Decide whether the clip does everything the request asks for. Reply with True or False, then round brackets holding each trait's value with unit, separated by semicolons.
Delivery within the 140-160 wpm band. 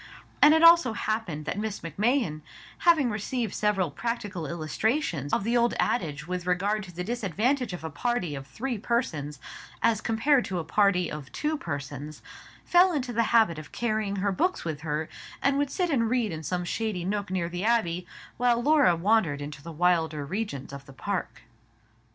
False (180 wpm)